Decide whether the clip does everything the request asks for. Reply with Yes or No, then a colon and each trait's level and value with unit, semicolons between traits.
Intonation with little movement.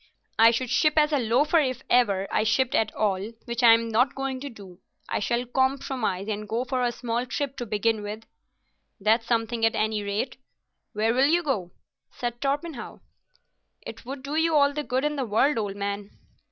No: average, 3.8 semitones